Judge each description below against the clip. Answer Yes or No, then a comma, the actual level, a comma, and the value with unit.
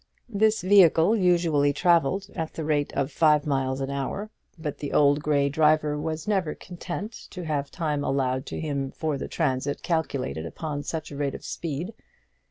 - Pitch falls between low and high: Yes, medium, 150 Hz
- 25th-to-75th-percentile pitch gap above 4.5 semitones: No, average, 3.2 semitones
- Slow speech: No, average, 175 wpm